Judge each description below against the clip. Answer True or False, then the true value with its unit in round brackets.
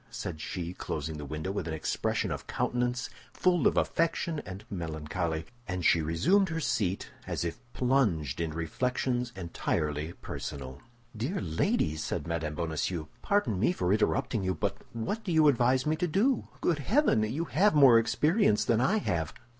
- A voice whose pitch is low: True (105 Hz)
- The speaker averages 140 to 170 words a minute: True (165 wpm)